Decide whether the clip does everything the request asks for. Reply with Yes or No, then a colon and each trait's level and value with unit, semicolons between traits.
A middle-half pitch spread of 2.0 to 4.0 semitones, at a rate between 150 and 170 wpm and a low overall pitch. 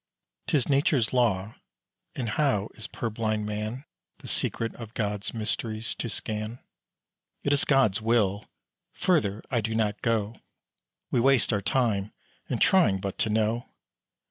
No: narrow, 2.4 semitones; average, 140 wpm; low, 110 Hz